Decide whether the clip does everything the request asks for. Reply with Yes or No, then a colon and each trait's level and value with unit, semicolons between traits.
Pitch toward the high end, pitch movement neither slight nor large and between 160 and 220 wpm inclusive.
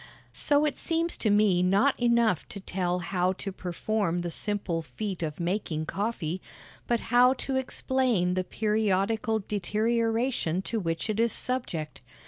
No: high, 205 Hz; average, 4.7 semitones; average, 145 wpm